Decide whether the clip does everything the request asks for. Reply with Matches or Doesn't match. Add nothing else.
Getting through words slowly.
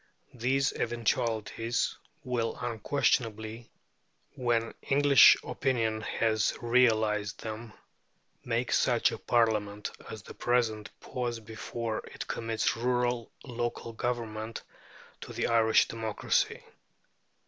Matches